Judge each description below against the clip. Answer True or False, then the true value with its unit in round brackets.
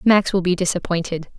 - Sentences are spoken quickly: False (175 wpm)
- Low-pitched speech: False (180 Hz)